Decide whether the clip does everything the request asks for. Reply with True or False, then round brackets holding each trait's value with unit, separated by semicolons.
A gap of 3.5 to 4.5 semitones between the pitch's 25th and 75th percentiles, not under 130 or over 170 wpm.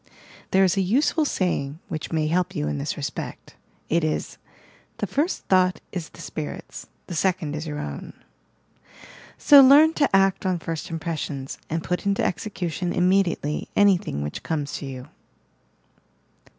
True (4.0 semitones; 150 wpm)